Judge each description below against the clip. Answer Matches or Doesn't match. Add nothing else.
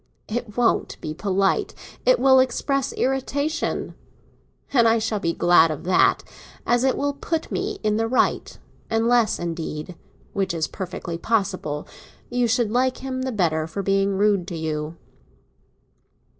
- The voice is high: Matches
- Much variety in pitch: Matches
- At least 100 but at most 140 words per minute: Matches